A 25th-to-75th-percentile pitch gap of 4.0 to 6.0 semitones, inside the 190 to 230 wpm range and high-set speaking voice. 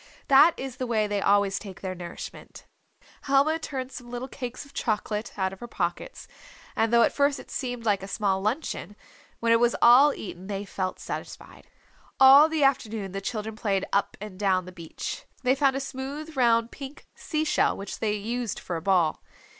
Yes: average, 5.2 semitones; average, 195 wpm; high, 230 Hz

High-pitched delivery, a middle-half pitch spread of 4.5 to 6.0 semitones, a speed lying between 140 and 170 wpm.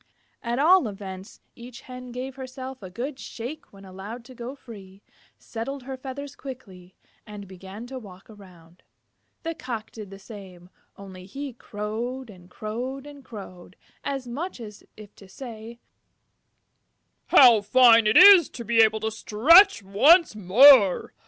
Yes: high, 230 Hz; average, 4.8 semitones; average, 145 wpm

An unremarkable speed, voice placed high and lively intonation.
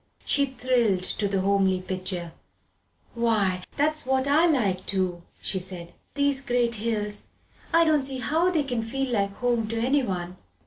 Yes: average, 155 wpm; high, 230 Hz; wide, 6.0 semitones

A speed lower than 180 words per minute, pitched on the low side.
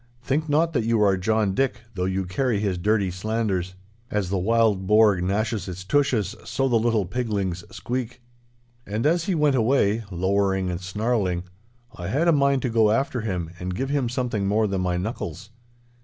No: average, 185 wpm; low, 105 Hz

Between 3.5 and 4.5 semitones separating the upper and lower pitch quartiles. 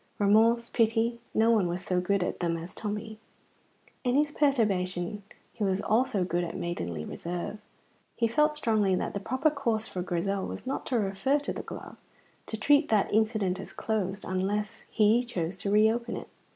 Yes: average, 3.8 semitones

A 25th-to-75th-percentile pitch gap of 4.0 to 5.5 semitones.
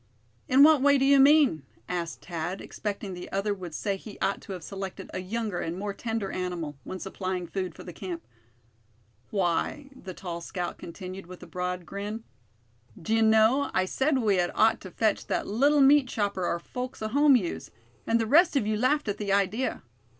Yes: average, 4.7 semitones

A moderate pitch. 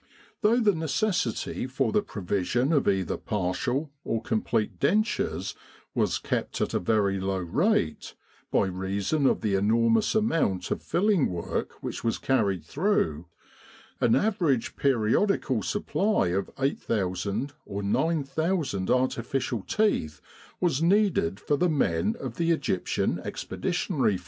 No: low, 120 Hz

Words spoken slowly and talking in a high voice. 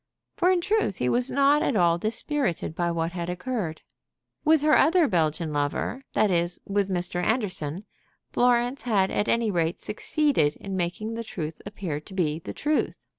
No: average, 175 wpm; high, 195 Hz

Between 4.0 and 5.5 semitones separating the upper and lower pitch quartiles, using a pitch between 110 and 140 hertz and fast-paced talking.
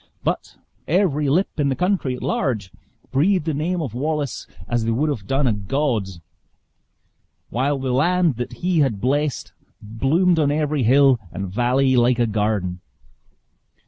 No: average, 4.5 semitones; low, 135 Hz; average, 155 wpm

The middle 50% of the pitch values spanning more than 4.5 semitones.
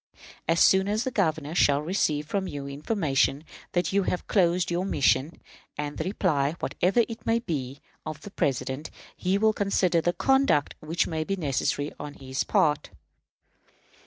Yes: average, 5.1 semitones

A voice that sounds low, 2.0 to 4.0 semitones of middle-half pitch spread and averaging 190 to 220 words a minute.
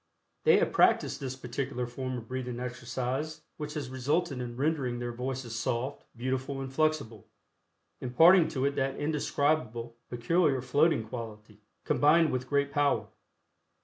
No: low, 130 Hz; average, 3.1 semitones; average, 140 wpm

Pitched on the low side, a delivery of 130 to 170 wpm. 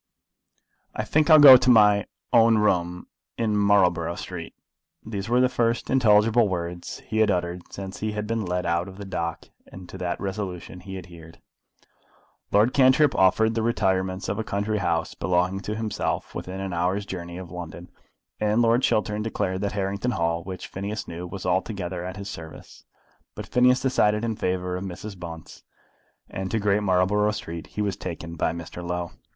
No: very low, 95 Hz; average, 180 wpm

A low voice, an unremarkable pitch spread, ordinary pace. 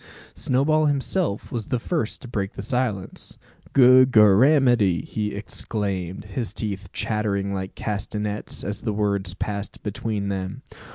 No: low, 105 Hz; average, 3.8 semitones; slow, 125 wpm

